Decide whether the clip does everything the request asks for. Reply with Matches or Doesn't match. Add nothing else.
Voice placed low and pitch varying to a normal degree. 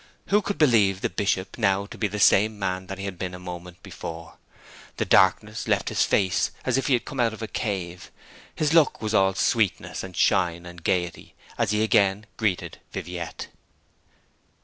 Matches